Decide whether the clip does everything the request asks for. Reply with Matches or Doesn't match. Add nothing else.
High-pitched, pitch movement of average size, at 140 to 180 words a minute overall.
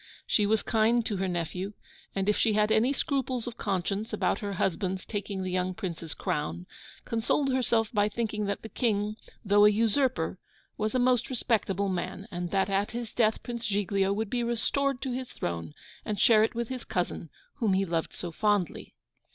Doesn't match